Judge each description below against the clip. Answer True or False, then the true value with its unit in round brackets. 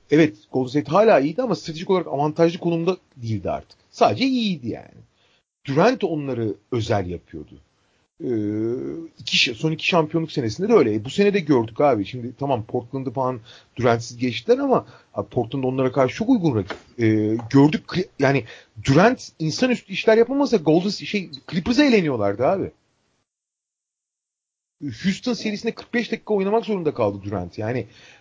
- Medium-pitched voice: True (150 Hz)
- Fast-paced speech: True (145 wpm)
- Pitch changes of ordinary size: False (8.5 semitones)